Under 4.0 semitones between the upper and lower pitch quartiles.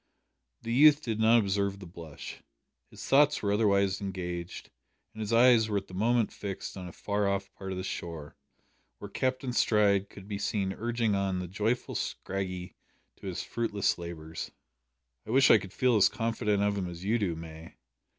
Yes: average, 3.5 semitones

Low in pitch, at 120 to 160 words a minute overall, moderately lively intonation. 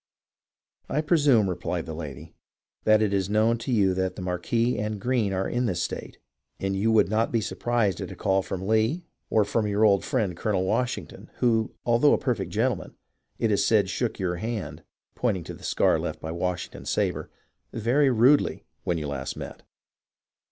No: low, 105 Hz; average, 185 wpm; average, 3.9 semitones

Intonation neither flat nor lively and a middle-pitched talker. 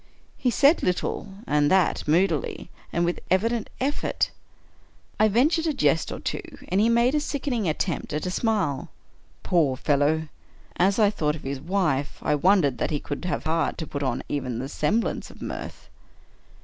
No: wide, 6.8 semitones; medium, 175 Hz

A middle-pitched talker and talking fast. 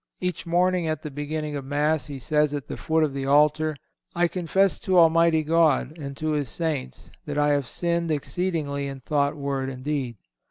No: medium, 150 Hz; average, 195 wpm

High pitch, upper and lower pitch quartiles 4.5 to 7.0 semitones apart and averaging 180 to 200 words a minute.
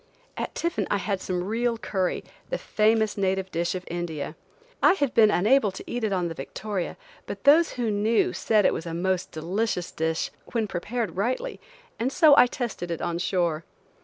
Yes: high, 200 Hz; average, 4.8 semitones; average, 190 wpm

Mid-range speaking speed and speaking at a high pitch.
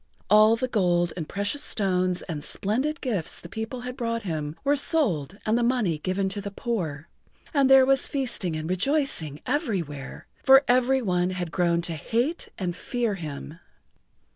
Yes: average, 165 wpm; high, 200 Hz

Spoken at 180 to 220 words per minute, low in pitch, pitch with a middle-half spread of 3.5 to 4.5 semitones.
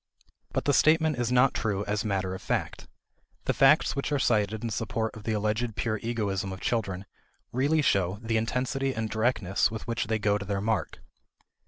No: average, 190 wpm; low, 110 Hz; average, 3.1 semitones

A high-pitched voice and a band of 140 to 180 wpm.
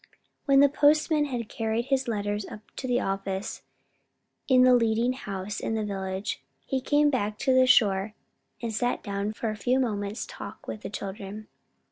Yes: high, 220 Hz; average, 175 wpm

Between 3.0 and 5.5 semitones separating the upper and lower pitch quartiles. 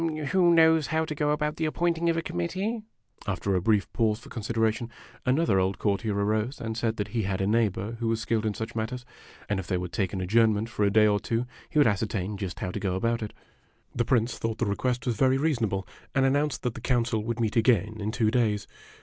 Yes: average, 3.9 semitones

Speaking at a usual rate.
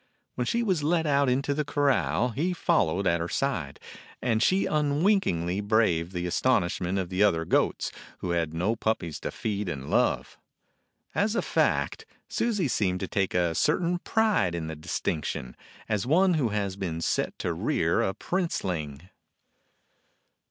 Yes: average, 160 wpm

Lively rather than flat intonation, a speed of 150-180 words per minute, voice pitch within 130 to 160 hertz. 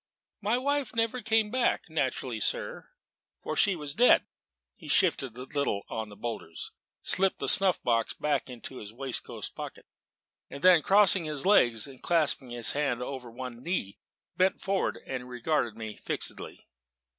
Yes: wide, 8.2 semitones; average, 155 wpm; medium, 140 Hz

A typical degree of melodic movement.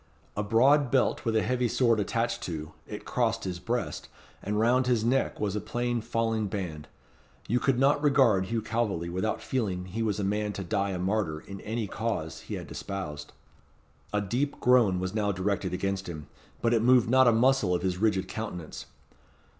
Yes: average, 4.2 semitones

